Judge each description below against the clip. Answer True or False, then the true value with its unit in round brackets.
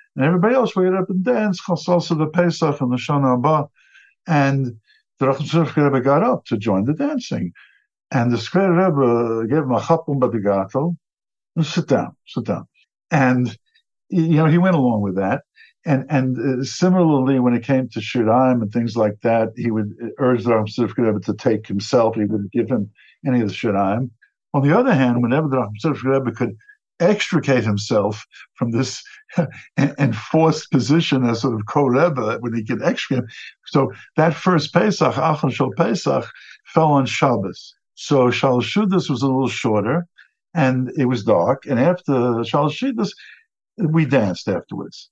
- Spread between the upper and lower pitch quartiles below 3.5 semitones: False (5.6 semitones)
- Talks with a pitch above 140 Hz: False (135 Hz)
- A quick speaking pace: False (170 wpm)